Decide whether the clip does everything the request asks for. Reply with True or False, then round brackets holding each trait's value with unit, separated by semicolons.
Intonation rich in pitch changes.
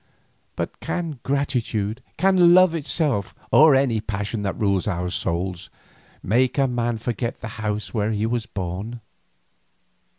False (5.0 semitones)